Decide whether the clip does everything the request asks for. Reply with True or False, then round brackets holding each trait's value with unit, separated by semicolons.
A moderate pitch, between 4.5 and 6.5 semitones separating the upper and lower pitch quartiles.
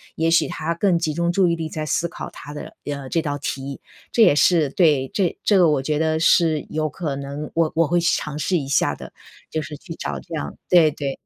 False (155 Hz; 2.8 semitones)